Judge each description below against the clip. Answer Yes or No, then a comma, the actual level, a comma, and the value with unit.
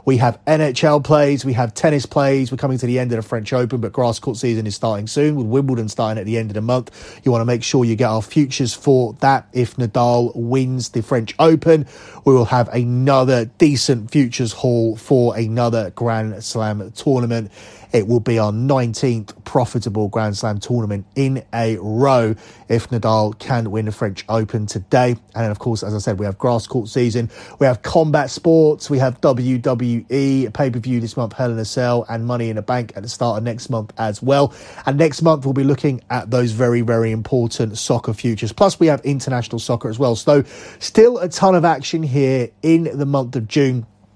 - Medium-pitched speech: No, low, 120 Hz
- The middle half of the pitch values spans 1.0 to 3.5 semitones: Yes, average, 3.2 semitones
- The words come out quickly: Yes, fast, 210 wpm